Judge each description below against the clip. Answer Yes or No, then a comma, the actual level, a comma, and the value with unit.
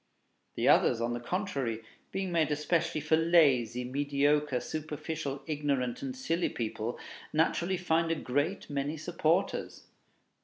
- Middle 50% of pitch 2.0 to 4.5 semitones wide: Yes, average, 3.5 semitones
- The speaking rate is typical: No, slow, 125 wpm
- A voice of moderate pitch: Yes, medium, 150 Hz